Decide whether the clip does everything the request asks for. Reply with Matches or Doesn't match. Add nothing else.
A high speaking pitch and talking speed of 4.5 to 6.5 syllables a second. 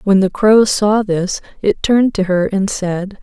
Doesn't match